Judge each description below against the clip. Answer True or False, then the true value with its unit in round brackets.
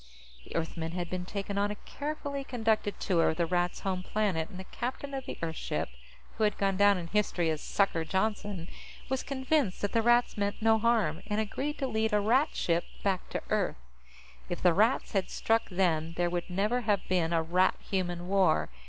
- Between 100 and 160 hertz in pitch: False (200 Hz)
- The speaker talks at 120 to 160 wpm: False (205 wpm)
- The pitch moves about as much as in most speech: True (4.0 semitones)